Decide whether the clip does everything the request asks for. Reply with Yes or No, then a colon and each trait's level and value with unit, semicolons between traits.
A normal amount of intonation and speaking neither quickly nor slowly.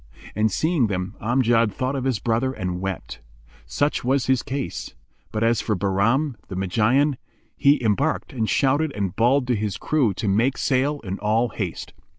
Yes: average, 4.5 semitones; average, 170 wpm